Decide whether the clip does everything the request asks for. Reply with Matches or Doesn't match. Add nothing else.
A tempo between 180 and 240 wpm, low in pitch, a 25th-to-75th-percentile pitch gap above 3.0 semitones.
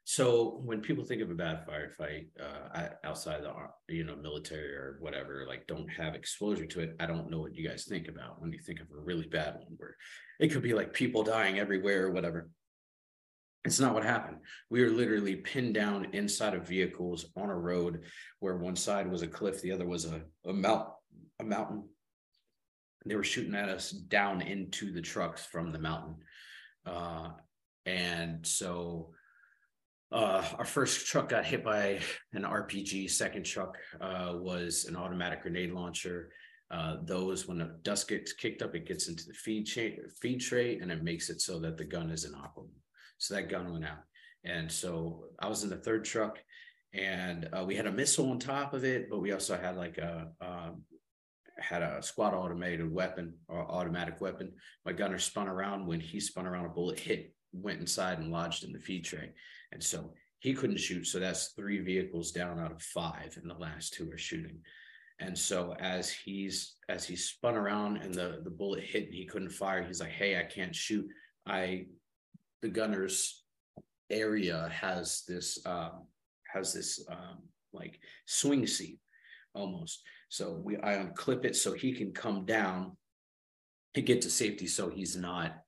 Matches